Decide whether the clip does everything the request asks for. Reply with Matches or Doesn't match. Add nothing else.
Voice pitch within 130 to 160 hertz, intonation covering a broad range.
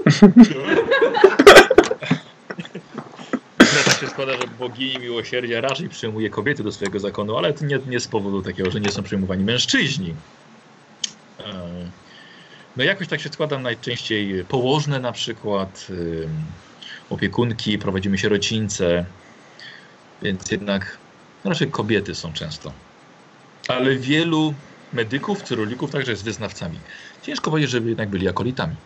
Doesn't match